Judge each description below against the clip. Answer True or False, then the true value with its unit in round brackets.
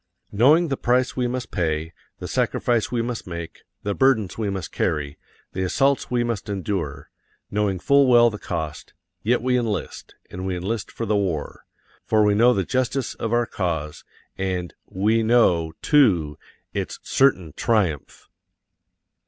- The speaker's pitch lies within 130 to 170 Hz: False (105 Hz)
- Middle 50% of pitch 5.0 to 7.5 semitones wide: True (5.3 semitones)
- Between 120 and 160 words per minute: True (155 wpm)